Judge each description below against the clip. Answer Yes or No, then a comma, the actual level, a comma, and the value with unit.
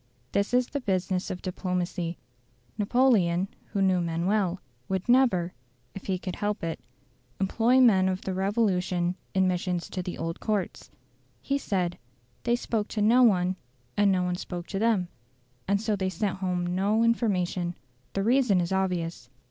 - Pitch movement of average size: Yes, average, 3.0 semitones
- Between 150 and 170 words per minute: Yes, average, 165 wpm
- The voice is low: No, high, 190 Hz